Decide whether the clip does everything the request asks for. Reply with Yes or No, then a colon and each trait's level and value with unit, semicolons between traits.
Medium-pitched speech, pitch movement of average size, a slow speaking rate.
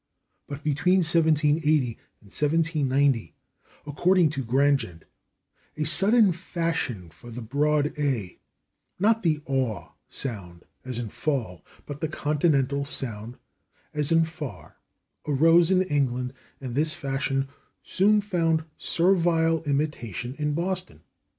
Yes: medium, 150 Hz; average, 4.0 semitones; slow, 115 wpm